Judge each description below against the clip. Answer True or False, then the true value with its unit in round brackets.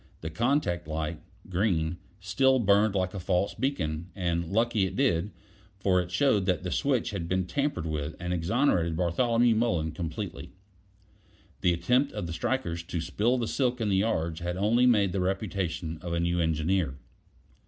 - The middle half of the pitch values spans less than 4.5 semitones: False (4.8 semitones)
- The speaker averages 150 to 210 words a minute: True (170 wpm)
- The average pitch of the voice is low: True (90 Hz)